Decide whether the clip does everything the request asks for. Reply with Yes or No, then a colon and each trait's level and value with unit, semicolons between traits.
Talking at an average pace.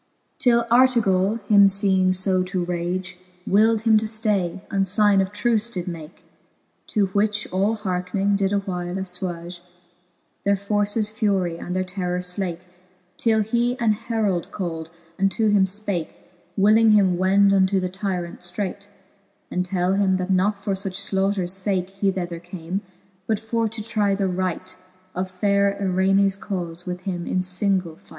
Yes: average, 160 wpm